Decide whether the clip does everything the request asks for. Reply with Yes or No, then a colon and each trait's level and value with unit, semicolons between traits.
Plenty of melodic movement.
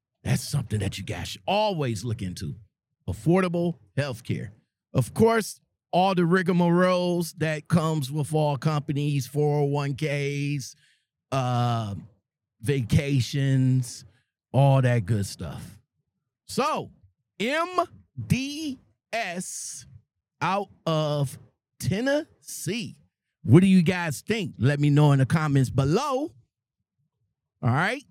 Yes: wide, 5.9 semitones